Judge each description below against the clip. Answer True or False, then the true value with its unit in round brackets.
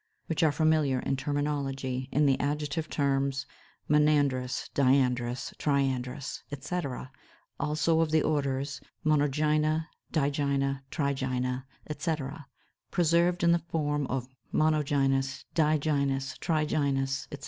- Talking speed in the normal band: False (105 wpm)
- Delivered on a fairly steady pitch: True (2.2 semitones)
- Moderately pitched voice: True (145 Hz)